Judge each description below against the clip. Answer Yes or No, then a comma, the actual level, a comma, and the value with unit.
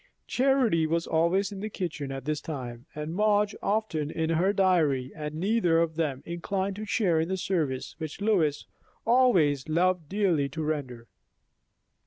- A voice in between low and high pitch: Yes, medium, 165 Hz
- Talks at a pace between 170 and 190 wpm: No, average, 160 wpm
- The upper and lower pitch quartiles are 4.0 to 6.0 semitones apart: Yes, average, 4.6 semitones